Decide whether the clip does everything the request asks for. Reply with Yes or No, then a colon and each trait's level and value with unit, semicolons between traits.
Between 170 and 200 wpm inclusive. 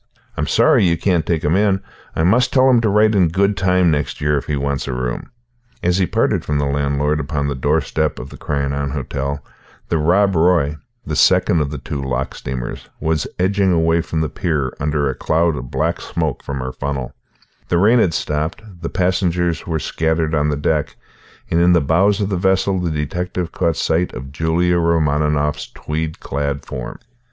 Yes: average, 195 wpm